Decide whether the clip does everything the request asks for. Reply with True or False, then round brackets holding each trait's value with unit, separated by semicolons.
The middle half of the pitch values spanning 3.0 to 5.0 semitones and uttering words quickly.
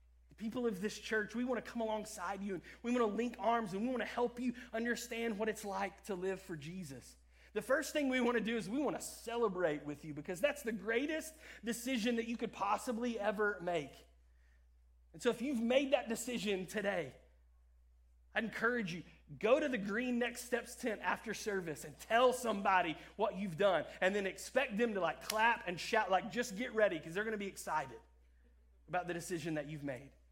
False (5.6 semitones; 210 wpm)